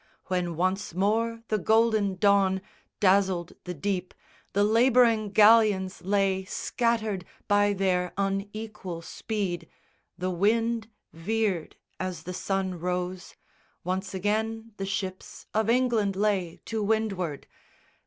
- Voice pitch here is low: No, high, 200 Hz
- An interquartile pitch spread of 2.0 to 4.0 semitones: Yes, average, 2.9 semitones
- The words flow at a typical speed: No, slow, 115 wpm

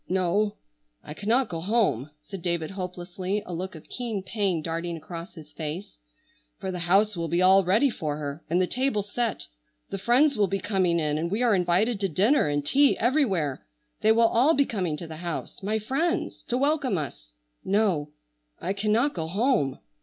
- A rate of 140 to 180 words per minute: No, average, 190 wpm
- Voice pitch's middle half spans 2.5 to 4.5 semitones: No, average, 5.0 semitones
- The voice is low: No, high, 190 Hz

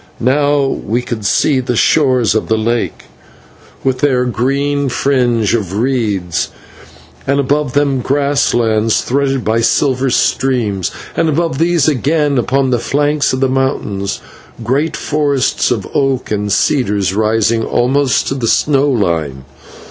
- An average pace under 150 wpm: Yes, average, 140 wpm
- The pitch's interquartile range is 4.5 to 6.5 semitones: No, average, 4.0 semitones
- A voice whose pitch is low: Yes, low, 130 Hz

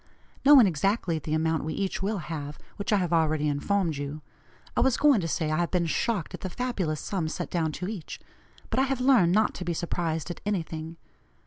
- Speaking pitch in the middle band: Yes, medium, 170 Hz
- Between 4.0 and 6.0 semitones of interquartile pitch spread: Yes, average, 4.3 semitones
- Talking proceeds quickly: Yes, fast, 215 wpm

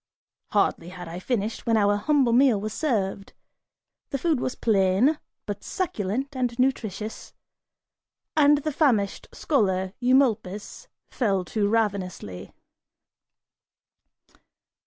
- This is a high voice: Yes, high, 220 Hz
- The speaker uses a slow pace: Yes, slow, 105 wpm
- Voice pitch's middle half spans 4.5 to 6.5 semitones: Yes, average, 5.3 semitones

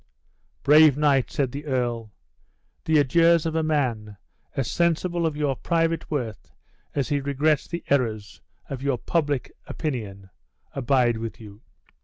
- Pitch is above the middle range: No, medium, 140 Hz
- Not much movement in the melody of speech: No, average, 4.6 semitones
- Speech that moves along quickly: No, average, 140 wpm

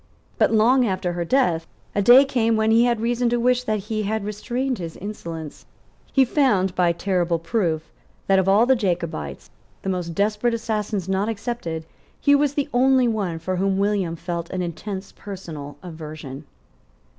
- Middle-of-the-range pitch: No, high, 200 Hz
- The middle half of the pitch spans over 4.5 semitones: Yes, wide, 5.4 semitones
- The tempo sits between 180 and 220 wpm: No, average, 170 wpm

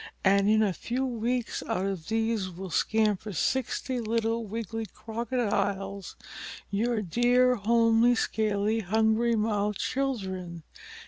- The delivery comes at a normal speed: No, slow, 115 wpm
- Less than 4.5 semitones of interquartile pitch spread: Yes, average, 2.7 semitones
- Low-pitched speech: No, high, 220 Hz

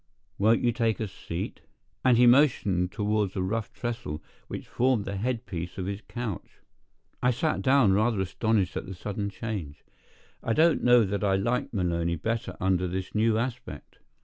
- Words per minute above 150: Yes, average, 175 wpm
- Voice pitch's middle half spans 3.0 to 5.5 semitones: Yes, average, 4.0 semitones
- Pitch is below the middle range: Yes, low, 105 Hz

